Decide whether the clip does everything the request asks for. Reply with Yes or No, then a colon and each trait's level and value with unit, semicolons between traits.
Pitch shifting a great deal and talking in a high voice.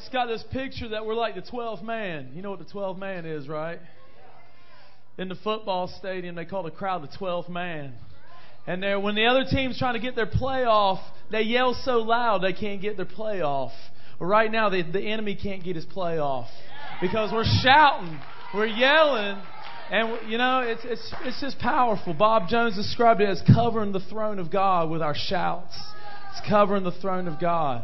No: average, 4.3 semitones; high, 200 Hz